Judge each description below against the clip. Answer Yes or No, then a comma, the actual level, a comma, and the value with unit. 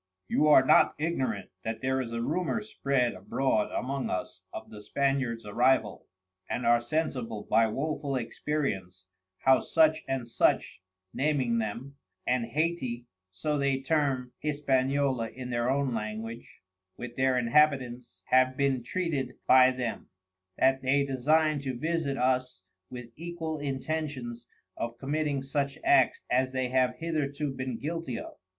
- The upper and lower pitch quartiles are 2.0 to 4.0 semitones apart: Yes, average, 3.2 semitones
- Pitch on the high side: No, low, 130 Hz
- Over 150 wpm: No, average, 140 wpm